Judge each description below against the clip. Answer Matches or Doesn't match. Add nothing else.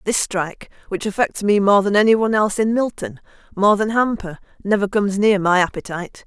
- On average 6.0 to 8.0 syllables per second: Matches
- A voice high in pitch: Matches